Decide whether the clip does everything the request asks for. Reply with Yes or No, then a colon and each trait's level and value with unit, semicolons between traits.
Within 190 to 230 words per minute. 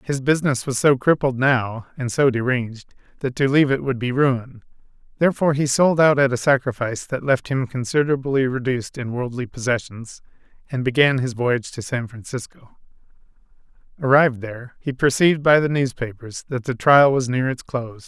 No: average, 175 wpm